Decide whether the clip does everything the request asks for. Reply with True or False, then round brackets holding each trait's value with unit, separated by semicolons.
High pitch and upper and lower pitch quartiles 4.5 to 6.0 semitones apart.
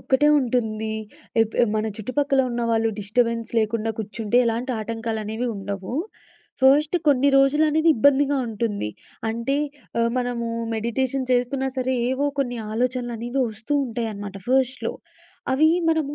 False (240 Hz; 3.2 semitones)